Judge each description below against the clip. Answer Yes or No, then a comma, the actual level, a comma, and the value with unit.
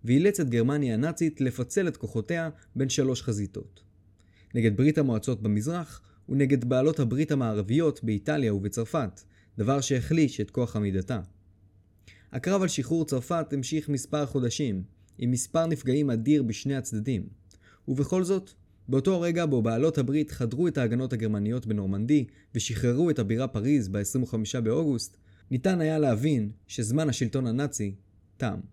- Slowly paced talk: No, average, 130 wpm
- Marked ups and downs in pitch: Yes, wide, 5.7 semitones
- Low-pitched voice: Yes, low, 125 Hz